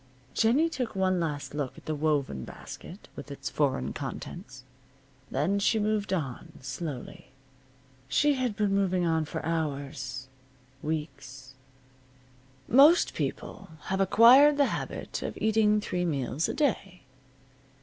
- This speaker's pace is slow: Yes, slow, 130 wpm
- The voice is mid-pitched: Yes, medium, 175 Hz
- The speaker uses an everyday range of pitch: No, wide, 7.4 semitones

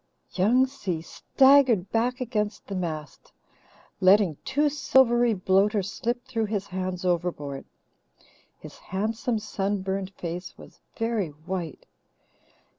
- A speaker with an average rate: No, slow, 110 wpm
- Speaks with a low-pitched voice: No, high, 200 Hz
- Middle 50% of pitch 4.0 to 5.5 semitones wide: Yes, average, 4.5 semitones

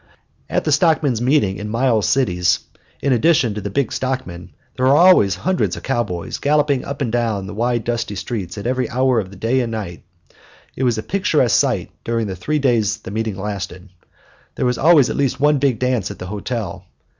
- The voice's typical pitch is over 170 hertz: No, low, 120 Hz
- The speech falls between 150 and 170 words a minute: No, average, 200 wpm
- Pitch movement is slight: No, average, 4.5 semitones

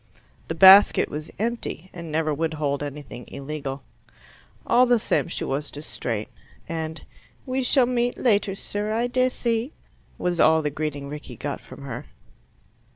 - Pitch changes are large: Yes, wide, 7.6 semitones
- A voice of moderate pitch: Yes, medium, 160 Hz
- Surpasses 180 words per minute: No, average, 150 wpm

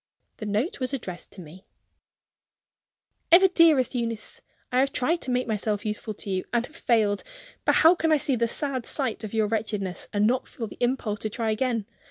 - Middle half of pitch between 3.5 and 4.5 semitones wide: Yes, average, 3.9 semitones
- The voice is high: Yes, high, 230 Hz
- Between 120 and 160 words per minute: No, average, 200 wpm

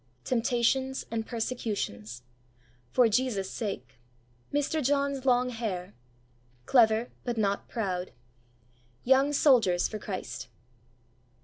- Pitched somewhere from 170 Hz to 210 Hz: No, high, 230 Hz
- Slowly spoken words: Yes, slow, 95 wpm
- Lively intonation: No, average, 4.9 semitones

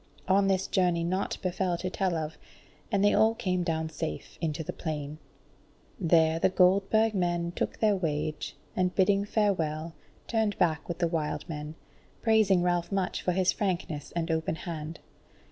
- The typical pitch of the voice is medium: Yes, medium, 175 Hz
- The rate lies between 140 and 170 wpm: Yes, average, 160 wpm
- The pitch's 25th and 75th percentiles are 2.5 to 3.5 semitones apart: Yes, average, 3.2 semitones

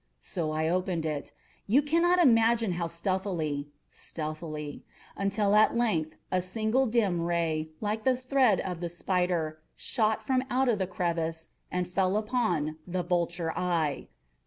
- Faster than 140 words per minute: No, slow, 135 wpm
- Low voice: No, medium, 180 Hz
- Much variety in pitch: No, average, 5.0 semitones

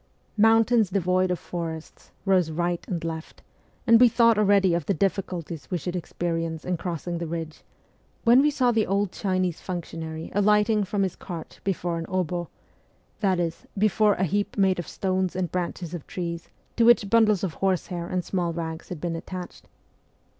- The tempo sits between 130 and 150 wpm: No, average, 175 wpm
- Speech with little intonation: No, average, 3.1 semitones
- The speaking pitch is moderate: Yes, medium, 180 Hz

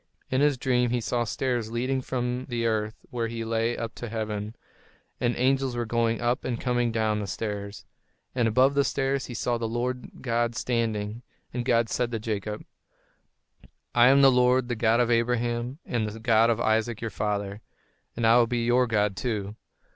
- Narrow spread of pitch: Yes, narrow, 1.8 semitones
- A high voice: No, low, 120 Hz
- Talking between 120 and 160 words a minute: No, average, 190 wpm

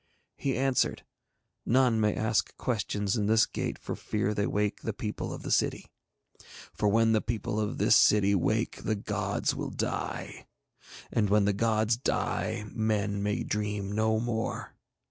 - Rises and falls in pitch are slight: Yes, narrow, 1.4 semitones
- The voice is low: Yes, low, 105 Hz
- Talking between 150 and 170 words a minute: Yes, average, 160 wpm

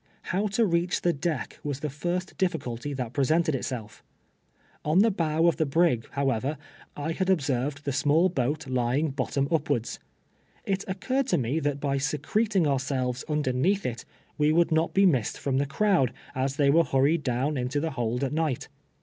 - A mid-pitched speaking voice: Yes, medium, 145 Hz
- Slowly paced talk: No, average, 180 wpm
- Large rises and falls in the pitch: No, average, 4.3 semitones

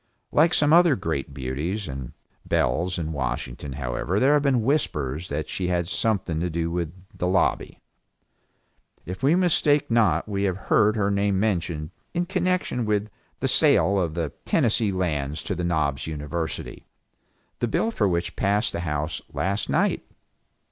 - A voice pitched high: No, very low, 90 Hz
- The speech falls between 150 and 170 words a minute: Yes, average, 160 wpm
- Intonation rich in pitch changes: Yes, wide, 5.8 semitones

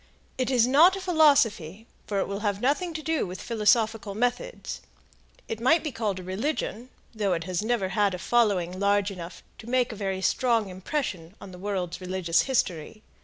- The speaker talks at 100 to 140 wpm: No, average, 185 wpm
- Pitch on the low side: No, high, 210 Hz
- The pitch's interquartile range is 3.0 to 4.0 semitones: No, average, 5.0 semitones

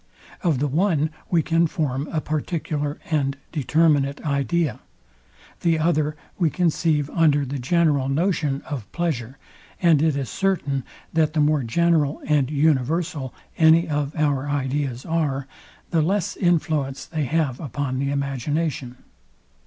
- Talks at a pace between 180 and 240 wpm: No, slow, 135 wpm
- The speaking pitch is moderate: Yes, medium, 150 Hz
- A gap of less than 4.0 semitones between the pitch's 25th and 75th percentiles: Yes, average, 2.9 semitones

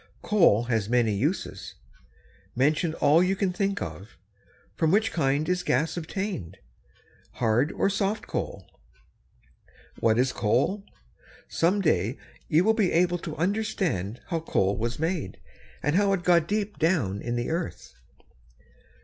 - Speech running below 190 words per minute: Yes, average, 140 wpm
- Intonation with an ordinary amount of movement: No, wide, 7.9 semitones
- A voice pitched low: No, medium, 160 Hz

